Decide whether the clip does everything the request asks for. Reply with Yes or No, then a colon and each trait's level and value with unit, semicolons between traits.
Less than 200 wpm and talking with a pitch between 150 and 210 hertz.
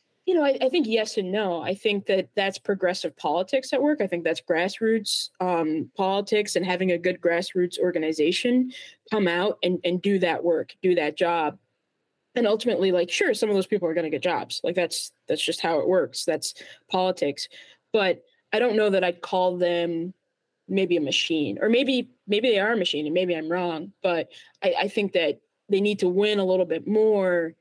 No: fast, 205 wpm; high, 190 Hz